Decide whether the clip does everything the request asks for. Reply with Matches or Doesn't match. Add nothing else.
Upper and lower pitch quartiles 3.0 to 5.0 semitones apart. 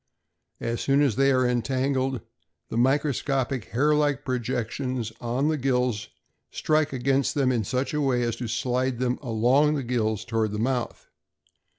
Doesn't match